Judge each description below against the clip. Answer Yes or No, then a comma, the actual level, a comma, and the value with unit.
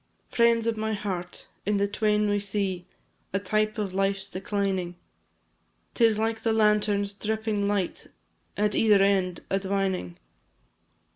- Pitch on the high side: Yes, high, 205 Hz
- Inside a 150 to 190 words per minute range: No, slow, 135 wpm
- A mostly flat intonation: Yes, narrow, 1.7 semitones